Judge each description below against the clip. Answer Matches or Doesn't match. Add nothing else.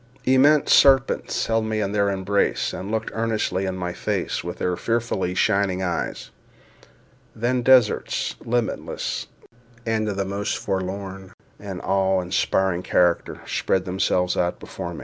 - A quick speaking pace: Doesn't match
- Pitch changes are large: Doesn't match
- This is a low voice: Matches